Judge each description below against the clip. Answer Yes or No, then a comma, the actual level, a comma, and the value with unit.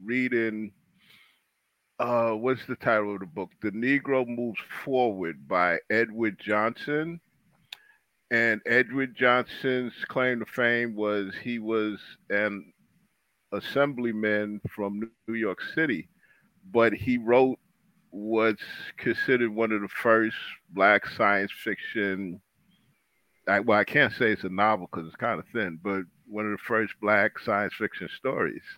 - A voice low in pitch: Yes, low, 115 Hz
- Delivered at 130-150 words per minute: Yes, slow, 135 wpm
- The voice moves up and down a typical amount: Yes, average, 3.1 semitones